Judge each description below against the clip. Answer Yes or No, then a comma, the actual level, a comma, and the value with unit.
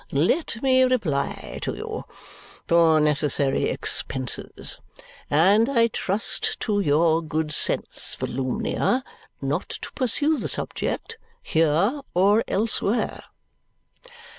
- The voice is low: No, medium, 180 Hz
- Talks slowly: Yes, slow, 100 wpm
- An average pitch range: No, wide, 7.3 semitones